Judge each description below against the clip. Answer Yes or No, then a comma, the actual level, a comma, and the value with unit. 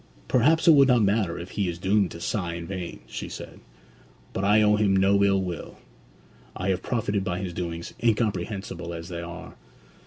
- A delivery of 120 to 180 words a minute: No, average, 190 wpm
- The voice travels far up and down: No, average, 3.2 semitones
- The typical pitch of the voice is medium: No, very low, 95 Hz